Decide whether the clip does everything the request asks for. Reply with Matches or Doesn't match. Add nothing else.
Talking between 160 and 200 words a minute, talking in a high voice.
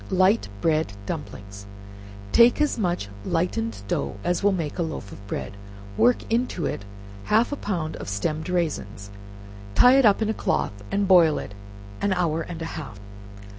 Doesn't match